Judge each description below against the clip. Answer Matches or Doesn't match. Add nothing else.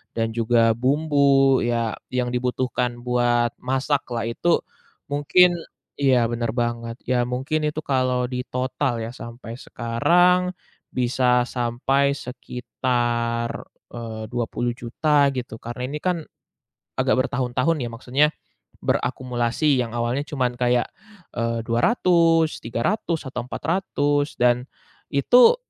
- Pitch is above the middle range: Doesn't match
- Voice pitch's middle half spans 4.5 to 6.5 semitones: Doesn't match